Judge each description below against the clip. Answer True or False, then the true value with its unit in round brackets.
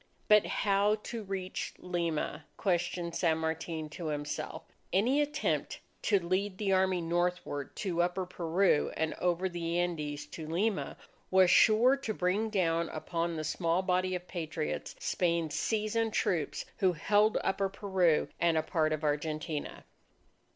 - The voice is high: False (175 Hz)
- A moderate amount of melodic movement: True (3.2 semitones)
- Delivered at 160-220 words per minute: False (145 wpm)